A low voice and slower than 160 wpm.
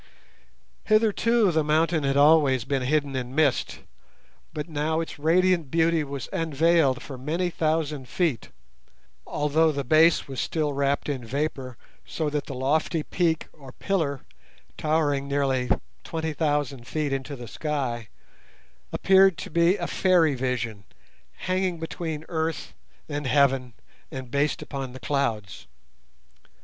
No: medium, 150 Hz; slow, 135 wpm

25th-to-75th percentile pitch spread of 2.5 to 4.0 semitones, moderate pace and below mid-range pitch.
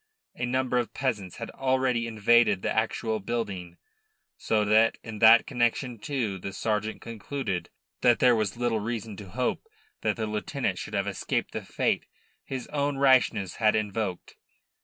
Yes: average, 2.8 semitones; average, 160 wpm; low, 115 Hz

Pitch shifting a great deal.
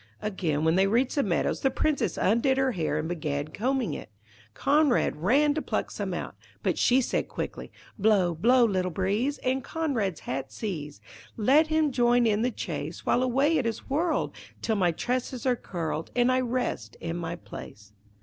Yes: wide, 7.1 semitones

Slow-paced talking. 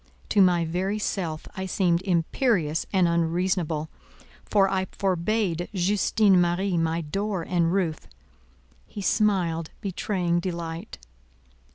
Yes: slow, 110 wpm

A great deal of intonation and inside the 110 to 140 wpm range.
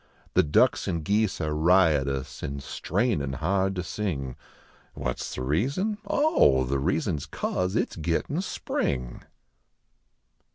Yes: wide, 6.1 semitones; slow, 135 wpm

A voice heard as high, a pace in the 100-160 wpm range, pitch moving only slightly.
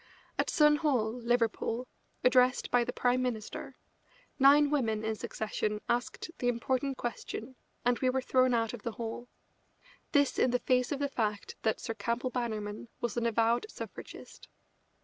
Yes: high, 245 Hz; average, 155 wpm; narrow, 2.1 semitones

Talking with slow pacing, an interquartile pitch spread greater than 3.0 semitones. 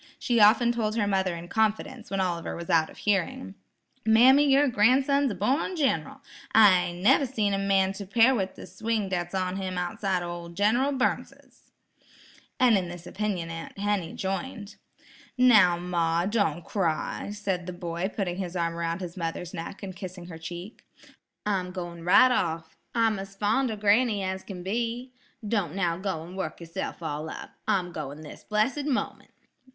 No: average, 175 wpm; average, 4.0 semitones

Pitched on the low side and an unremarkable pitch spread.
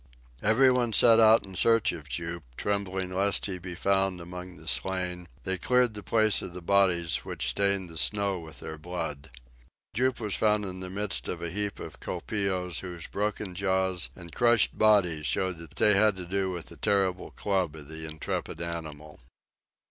Yes: very low, 95 Hz; average, 3.1 semitones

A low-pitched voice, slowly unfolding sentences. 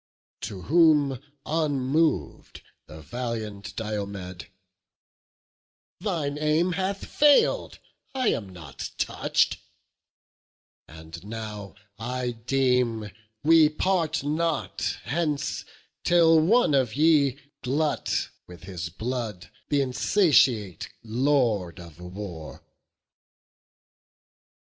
Yes: low, 125 Hz; slow, 85 wpm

